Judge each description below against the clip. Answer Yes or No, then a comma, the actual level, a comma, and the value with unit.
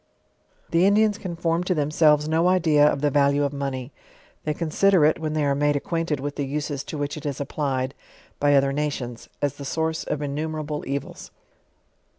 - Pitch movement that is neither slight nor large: No, narrow, 2.2 semitones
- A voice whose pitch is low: No, medium, 150 Hz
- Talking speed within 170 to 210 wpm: Yes, average, 185 wpm